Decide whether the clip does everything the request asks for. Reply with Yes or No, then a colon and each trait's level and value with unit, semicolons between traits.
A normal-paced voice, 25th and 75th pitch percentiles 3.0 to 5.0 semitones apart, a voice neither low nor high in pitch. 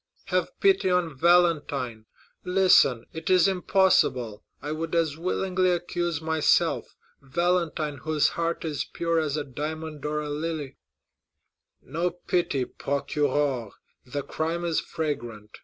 No: slow, 125 wpm; average, 3.3 semitones; medium, 160 Hz